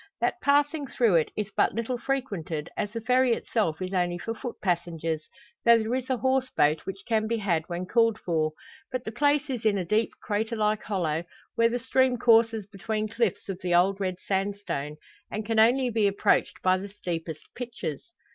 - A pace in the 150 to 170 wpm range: No, average, 195 wpm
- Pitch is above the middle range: Yes, high, 215 Hz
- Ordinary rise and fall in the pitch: Yes, average, 4.6 semitones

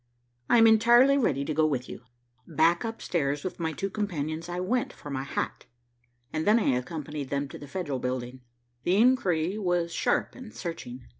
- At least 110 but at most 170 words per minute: No, average, 190 wpm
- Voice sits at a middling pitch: Yes, medium, 165 Hz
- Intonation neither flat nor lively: No, wide, 6.6 semitones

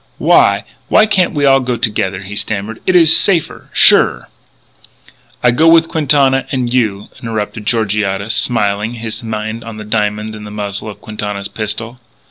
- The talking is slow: No, average, 165 wpm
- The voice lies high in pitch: No, low, 110 Hz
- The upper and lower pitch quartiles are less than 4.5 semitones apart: Yes, average, 3.6 semitones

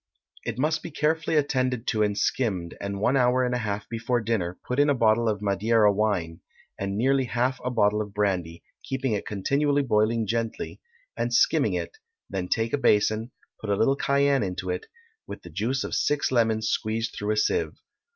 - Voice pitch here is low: Yes, low, 115 Hz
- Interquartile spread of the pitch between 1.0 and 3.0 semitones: No, average, 3.9 semitones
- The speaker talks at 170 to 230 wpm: Yes, average, 190 wpm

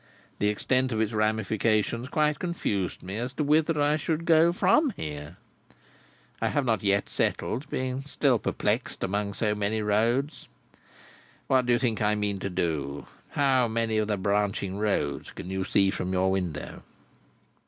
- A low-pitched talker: Yes, low, 110 Hz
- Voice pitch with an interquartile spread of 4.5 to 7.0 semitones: Yes, average, 4.9 semitones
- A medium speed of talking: Yes, average, 165 wpm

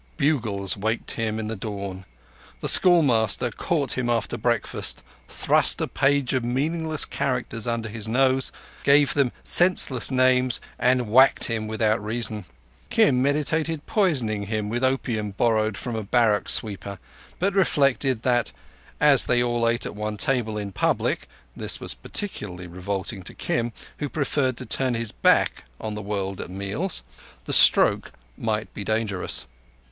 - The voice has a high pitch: No, low, 115 Hz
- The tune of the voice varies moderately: Yes, average, 3.9 semitones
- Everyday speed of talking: Yes, average, 150 wpm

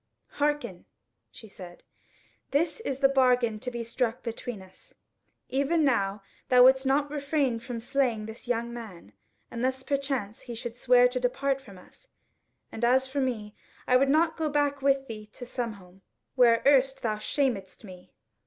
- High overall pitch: Yes, very high, 250 Hz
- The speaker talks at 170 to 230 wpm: No, average, 160 wpm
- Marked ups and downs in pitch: No, average, 3.4 semitones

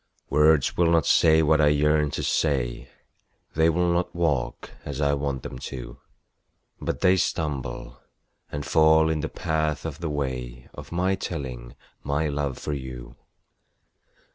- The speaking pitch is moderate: No, very low, 75 Hz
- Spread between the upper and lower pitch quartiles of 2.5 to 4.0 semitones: Yes, average, 2.9 semitones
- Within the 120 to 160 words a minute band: Yes, average, 150 wpm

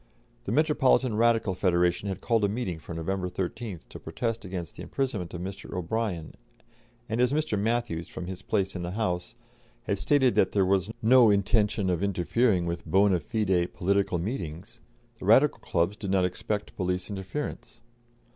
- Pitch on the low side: Yes, low, 100 Hz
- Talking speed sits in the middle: Yes, average, 165 wpm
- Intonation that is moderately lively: Yes, average, 4.0 semitones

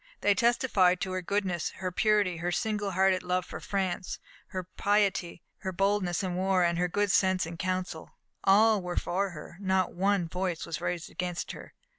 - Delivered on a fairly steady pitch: Yes, narrow, 2.0 semitones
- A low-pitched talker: No, medium, 185 Hz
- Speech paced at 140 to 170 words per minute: No, average, 180 wpm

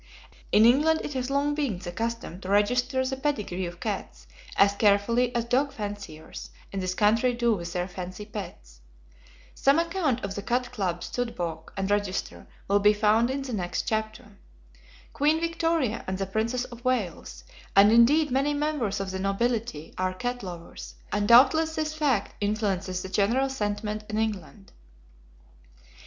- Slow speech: No, average, 165 wpm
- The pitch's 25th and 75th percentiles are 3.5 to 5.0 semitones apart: Yes, average, 4.7 semitones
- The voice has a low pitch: No, high, 215 Hz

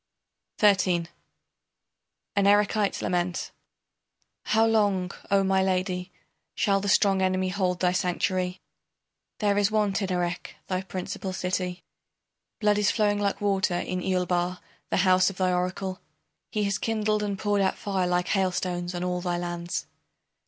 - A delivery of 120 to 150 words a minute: Yes, average, 145 wpm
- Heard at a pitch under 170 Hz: No, medium, 185 Hz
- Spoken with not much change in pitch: Yes, narrow, 1.9 semitones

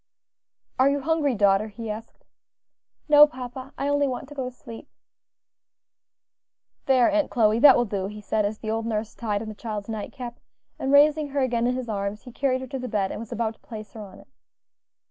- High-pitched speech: Yes, high, 235 Hz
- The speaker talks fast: Yes, fast, 215 wpm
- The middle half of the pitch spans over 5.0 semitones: No, average, 3.9 semitones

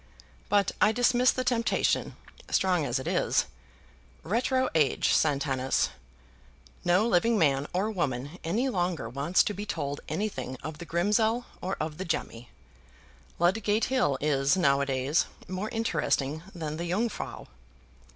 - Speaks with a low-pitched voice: No, medium, 175 Hz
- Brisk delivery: No, average, 140 wpm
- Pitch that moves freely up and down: Yes, wide, 7.0 semitones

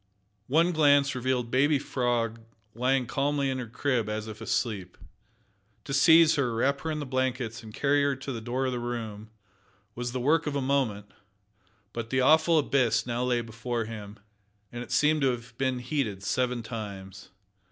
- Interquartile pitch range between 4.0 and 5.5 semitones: No, average, 3.3 semitones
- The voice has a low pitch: Yes, low, 125 Hz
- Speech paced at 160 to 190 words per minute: Yes, average, 180 wpm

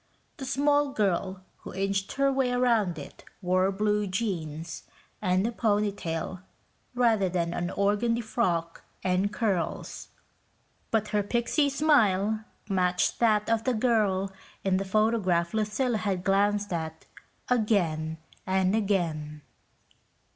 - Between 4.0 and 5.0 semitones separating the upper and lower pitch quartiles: No, average, 3.6 semitones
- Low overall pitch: No, high, 200 Hz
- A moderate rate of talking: No, slow, 125 wpm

